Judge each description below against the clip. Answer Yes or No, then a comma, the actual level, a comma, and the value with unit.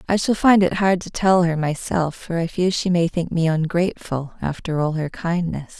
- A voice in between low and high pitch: Yes, medium, 170 Hz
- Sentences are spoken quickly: Yes, fast, 220 wpm